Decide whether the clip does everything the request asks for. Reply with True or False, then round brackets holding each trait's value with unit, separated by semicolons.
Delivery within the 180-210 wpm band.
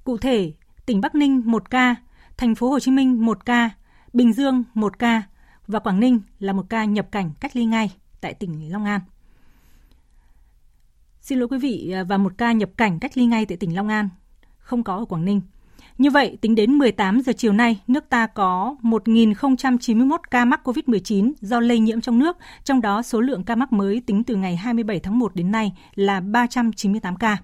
True (200 wpm)